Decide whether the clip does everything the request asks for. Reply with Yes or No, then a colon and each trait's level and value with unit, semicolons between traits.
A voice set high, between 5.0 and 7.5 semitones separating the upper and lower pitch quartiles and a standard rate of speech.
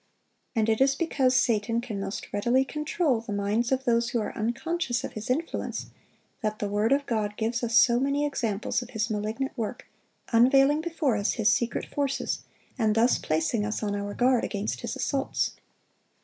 No: high, 235 Hz; average, 3.9 semitones; average, 180 wpm